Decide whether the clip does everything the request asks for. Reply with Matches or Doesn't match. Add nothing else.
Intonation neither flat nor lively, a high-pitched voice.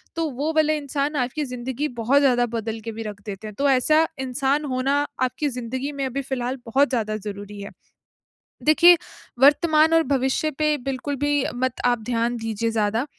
Matches